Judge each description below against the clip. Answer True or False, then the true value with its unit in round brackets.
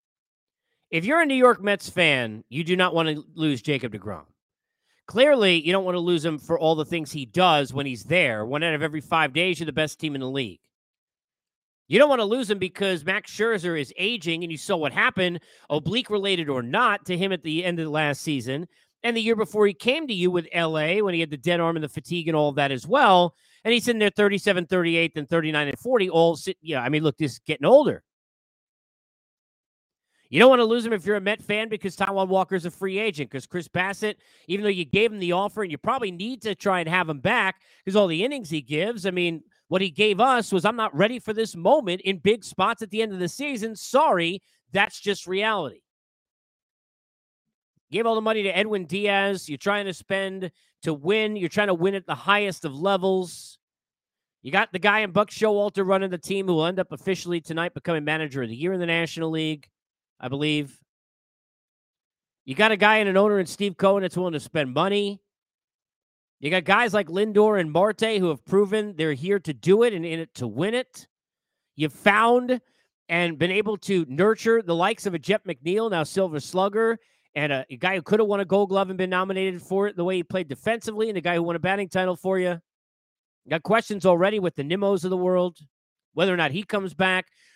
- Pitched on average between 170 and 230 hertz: True (185 Hz)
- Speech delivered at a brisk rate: True (230 wpm)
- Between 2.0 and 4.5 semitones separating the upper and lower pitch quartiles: True (4.2 semitones)